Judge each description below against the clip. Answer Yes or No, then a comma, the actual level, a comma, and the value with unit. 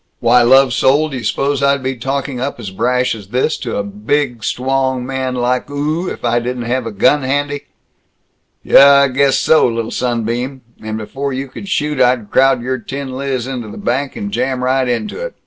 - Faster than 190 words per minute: Yes, average, 200 wpm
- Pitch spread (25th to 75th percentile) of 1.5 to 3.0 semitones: Yes, narrow, 2.5 semitones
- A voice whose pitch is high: No, low, 130 Hz